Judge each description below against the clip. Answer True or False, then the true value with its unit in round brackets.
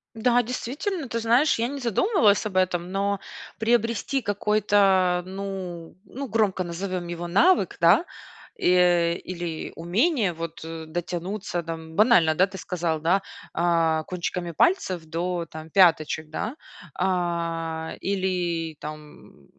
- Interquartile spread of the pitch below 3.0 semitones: False (4.1 semitones)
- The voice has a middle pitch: True (180 Hz)